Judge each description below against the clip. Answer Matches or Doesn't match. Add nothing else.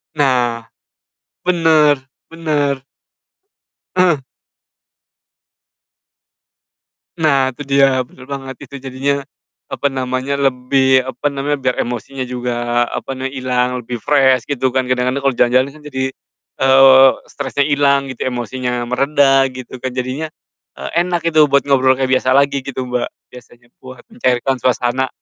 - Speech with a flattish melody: Matches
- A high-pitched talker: Doesn't match